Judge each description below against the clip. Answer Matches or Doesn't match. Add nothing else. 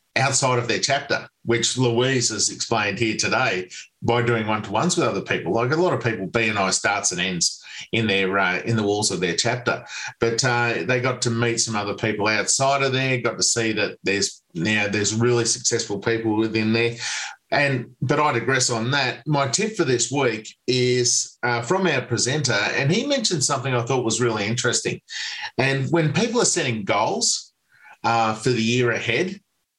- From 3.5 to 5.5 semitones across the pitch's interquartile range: Doesn't match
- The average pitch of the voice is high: Doesn't match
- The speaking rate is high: Doesn't match